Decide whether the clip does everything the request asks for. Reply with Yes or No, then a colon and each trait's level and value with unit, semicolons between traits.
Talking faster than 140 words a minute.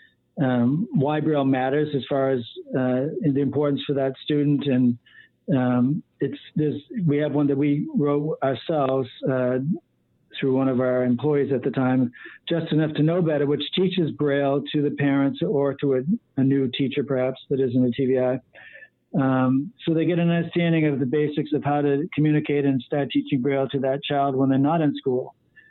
Yes: average, 185 wpm